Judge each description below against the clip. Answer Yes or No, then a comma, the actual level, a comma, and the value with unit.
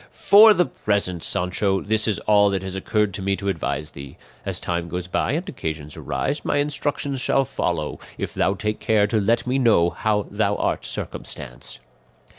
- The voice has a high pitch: No, low, 105 Hz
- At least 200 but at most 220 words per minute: No, average, 185 wpm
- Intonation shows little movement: No, average, 4.6 semitones